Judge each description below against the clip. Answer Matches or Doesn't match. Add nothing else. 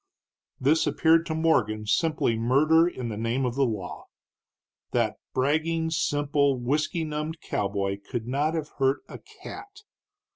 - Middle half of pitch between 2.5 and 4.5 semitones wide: Doesn't match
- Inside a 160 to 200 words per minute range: Doesn't match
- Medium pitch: Matches